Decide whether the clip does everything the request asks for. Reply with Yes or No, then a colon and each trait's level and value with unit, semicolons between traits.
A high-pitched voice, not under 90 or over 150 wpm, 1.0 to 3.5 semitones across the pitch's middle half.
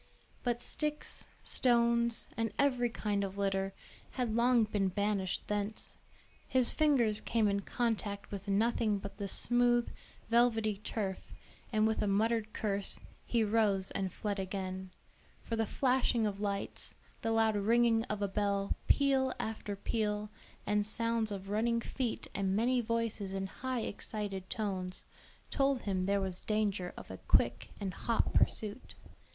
Yes: high, 215 Hz; average, 145 wpm; average, 2.8 semitones